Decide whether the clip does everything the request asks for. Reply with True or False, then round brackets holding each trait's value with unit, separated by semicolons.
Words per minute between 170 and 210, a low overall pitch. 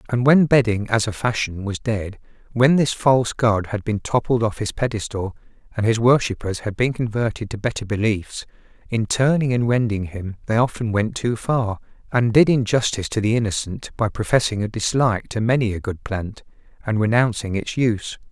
True (185 wpm; 115 Hz)